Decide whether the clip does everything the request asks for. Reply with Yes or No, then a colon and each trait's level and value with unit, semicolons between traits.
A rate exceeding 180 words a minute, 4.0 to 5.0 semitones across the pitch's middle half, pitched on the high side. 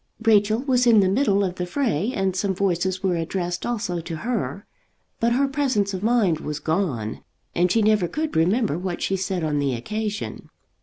Yes: average, 190 wpm; average, 4.3 semitones; high, 195 Hz